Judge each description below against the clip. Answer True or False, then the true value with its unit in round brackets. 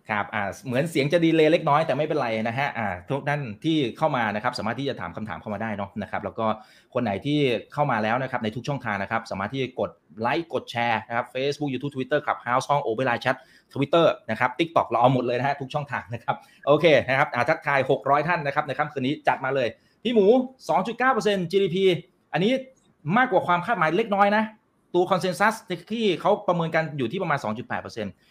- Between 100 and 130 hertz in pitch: False (140 Hz)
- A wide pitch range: True (6.7 semitones)